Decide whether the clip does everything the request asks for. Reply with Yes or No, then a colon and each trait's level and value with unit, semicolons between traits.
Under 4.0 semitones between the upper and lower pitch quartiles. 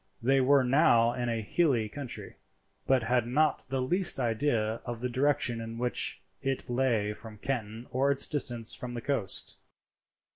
Yes: average, 2.9 semitones